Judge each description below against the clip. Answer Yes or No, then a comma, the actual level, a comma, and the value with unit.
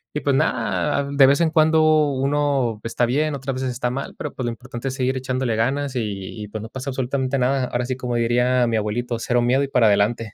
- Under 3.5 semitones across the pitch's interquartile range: Yes, average, 2.7 semitones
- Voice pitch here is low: Yes, low, 130 Hz